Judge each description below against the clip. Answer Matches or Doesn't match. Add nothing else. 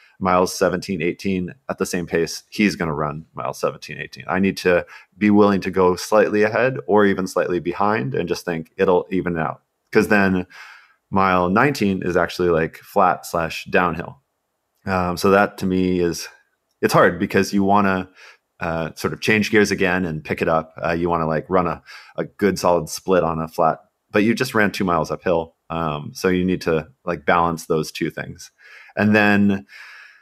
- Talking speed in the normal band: Matches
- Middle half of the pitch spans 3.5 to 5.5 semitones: Doesn't match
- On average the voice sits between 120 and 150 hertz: Doesn't match